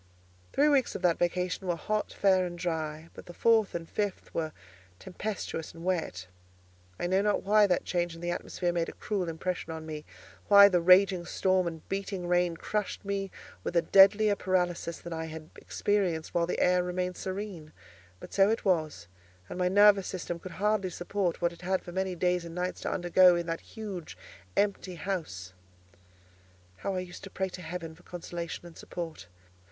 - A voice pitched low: No, medium, 180 Hz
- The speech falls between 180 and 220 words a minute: Yes, average, 190 wpm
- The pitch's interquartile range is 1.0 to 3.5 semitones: Yes, narrow, 2.4 semitones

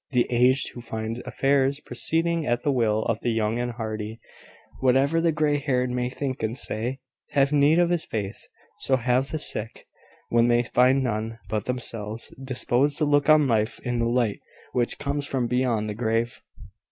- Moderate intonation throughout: Yes, average, 3.5 semitones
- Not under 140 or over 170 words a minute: No, average, 180 wpm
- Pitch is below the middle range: Yes, low, 125 Hz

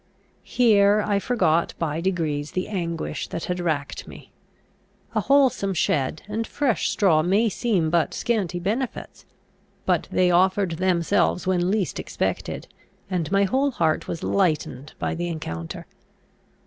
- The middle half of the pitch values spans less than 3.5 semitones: No, average, 3.8 semitones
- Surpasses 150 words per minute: No, slow, 135 wpm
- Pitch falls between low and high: Yes, medium, 180 Hz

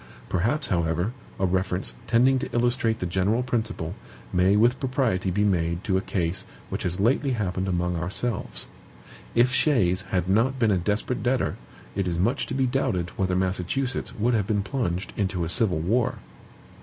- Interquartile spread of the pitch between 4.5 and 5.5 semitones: Yes, average, 5.0 semitones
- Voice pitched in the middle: No, low, 100 Hz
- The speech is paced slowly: No, average, 170 wpm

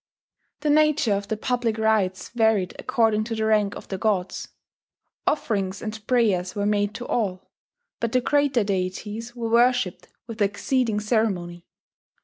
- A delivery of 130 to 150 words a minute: Yes, average, 145 wpm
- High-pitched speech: Yes, high, 220 Hz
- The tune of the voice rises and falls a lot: No, average, 3.0 semitones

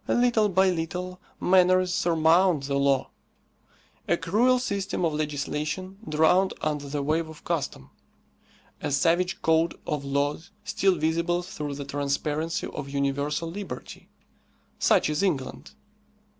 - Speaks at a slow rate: Yes, slow, 125 wpm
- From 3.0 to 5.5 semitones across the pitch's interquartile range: Yes, average, 4.0 semitones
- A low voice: No, medium, 160 Hz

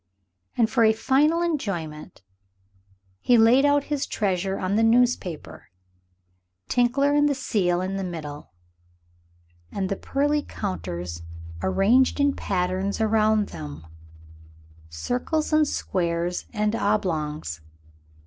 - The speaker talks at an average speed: No, slow, 110 wpm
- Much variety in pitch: Yes, wide, 7.1 semitones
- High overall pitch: Yes, high, 210 Hz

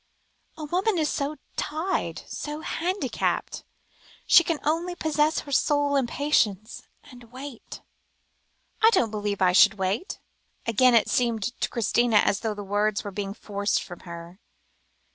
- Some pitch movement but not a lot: No, wide, 6.7 semitones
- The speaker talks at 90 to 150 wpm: Yes, average, 145 wpm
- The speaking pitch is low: No, high, 245 Hz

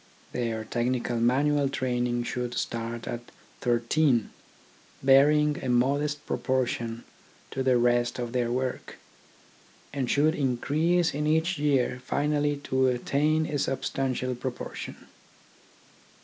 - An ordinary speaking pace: No, slow, 115 wpm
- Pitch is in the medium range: No, low, 130 Hz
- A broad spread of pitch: No, average, 3.2 semitones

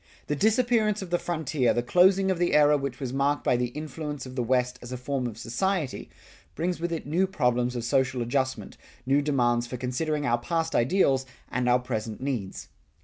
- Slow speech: No, average, 200 wpm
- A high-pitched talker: No, low, 135 Hz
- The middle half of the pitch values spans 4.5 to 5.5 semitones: Yes, average, 4.8 semitones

